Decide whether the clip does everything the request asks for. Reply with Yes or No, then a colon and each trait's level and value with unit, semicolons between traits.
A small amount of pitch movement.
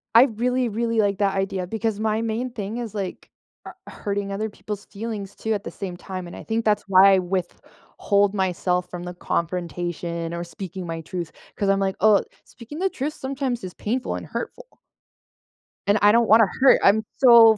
No: average, 3.5 semitones